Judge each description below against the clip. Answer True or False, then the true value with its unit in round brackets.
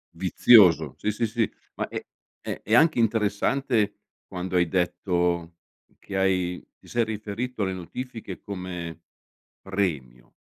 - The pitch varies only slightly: False (4.1 semitones)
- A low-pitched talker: True (100 Hz)